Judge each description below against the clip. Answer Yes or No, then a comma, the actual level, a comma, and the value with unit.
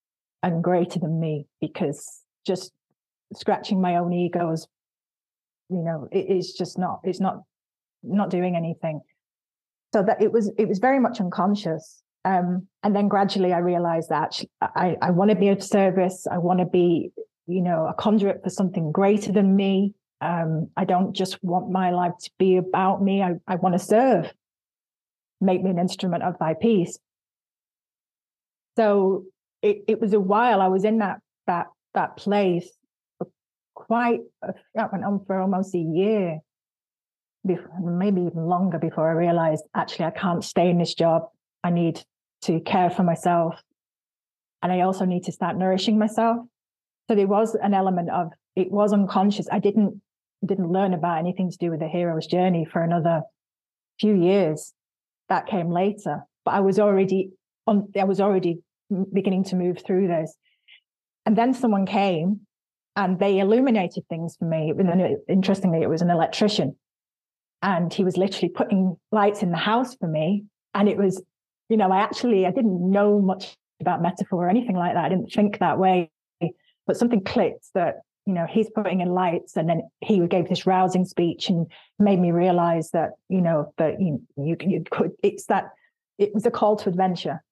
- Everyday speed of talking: Yes, average, 175 wpm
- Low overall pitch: No, medium, 185 Hz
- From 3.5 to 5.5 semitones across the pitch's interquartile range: No, average, 2.7 semitones